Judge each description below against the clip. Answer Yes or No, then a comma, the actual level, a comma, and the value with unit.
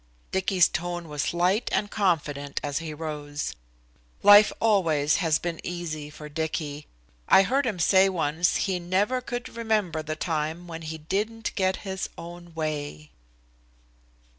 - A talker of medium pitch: Yes, medium, 170 Hz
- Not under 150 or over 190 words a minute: No, average, 140 wpm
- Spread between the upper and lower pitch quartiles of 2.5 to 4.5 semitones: Yes, average, 3.9 semitones